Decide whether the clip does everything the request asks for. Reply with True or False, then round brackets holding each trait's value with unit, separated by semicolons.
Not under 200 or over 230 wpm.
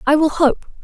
True (215 wpm)